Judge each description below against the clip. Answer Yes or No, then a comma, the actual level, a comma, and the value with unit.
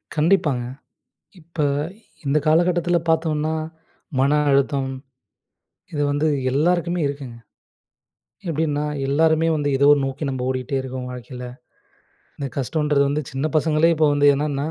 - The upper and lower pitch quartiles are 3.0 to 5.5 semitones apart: No, narrow, 2.5 semitones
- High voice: No, medium, 145 Hz